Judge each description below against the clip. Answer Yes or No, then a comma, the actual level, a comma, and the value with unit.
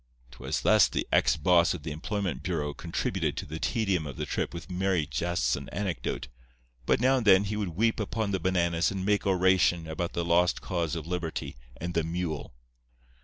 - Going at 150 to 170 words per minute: No, average, 195 wpm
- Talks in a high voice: No, very low, 90 Hz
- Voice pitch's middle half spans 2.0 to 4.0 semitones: Yes, average, 2.9 semitones